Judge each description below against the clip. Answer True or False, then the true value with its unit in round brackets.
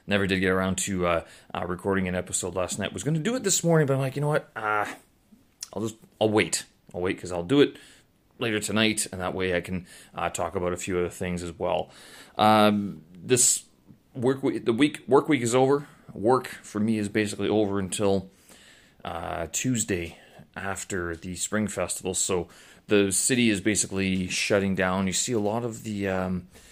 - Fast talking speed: False (195 wpm)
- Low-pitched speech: True (100 Hz)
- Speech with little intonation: False (3.4 semitones)